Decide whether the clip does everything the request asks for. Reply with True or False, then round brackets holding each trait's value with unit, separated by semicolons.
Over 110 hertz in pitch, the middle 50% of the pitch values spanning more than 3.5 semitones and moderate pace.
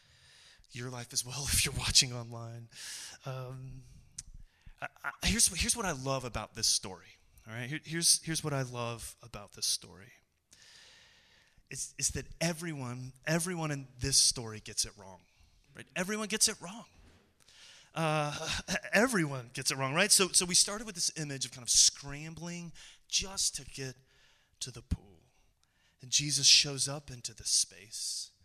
True (135 Hz; 5.4 semitones; 160 wpm)